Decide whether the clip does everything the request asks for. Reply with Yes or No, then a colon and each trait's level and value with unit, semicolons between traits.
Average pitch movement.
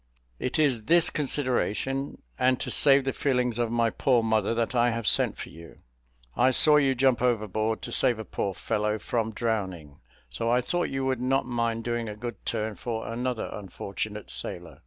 Yes: average, 3.0 semitones